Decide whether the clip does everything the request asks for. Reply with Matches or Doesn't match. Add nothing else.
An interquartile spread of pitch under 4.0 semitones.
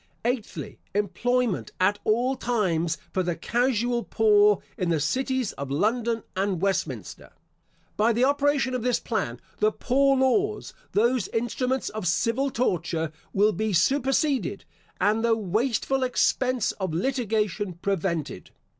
Doesn't match